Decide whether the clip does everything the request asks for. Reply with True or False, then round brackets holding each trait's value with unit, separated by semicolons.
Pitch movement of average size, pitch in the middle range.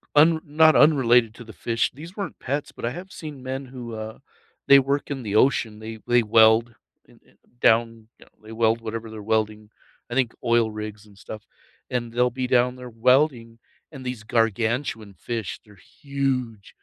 False (3.0 semitones; 120 Hz)